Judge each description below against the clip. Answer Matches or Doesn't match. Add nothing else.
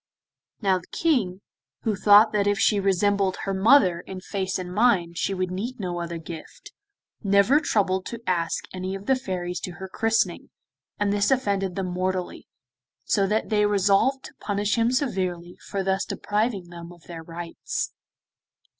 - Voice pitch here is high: Matches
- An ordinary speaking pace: Matches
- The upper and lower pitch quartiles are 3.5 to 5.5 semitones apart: Doesn't match